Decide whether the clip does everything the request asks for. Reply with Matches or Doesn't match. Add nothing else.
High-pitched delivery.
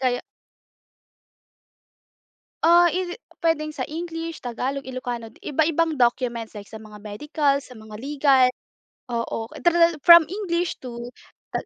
Matches